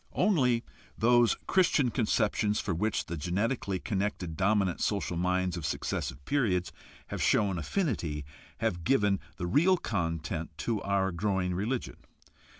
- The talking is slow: Yes, slow, 130 wpm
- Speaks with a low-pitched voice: Yes, low, 100 Hz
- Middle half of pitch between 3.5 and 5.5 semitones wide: Yes, average, 4.8 semitones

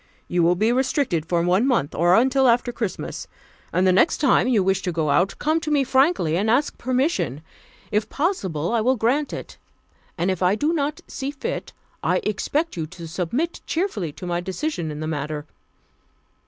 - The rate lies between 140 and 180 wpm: No, average, 195 wpm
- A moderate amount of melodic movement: No, wide, 8.0 semitones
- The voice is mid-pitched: No, high, 215 Hz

